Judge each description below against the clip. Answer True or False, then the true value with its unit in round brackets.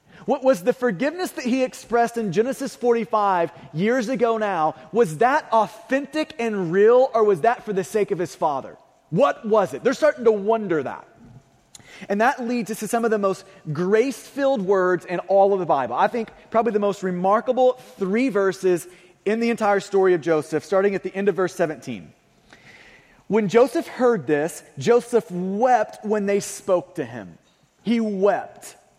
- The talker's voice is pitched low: False (210 Hz)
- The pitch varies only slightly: False (4.2 semitones)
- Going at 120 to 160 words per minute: False (180 wpm)